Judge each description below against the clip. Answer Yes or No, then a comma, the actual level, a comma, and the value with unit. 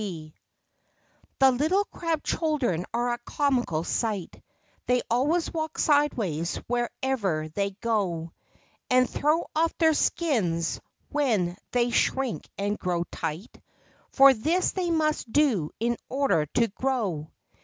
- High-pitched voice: Yes, high, 240 Hz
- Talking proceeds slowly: Yes, slow, 125 wpm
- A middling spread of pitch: No, wide, 8.0 semitones